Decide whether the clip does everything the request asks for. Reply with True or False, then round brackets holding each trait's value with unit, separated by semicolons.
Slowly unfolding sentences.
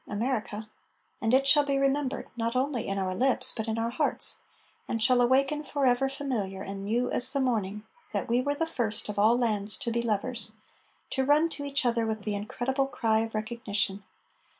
False (195 wpm)